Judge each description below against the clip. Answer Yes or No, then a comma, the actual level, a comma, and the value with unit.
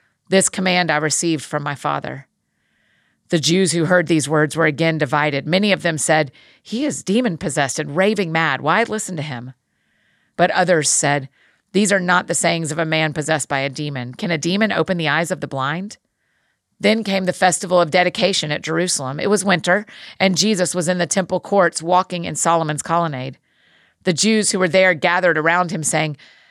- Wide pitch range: No, average, 3.4 semitones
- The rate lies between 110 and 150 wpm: No, average, 195 wpm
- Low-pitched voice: No, medium, 170 Hz